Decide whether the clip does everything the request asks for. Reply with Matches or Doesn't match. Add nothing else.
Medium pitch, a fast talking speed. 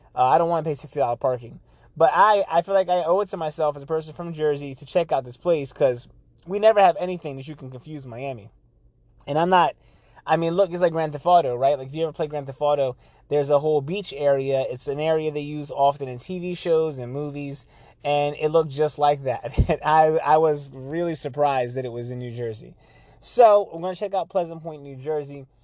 Matches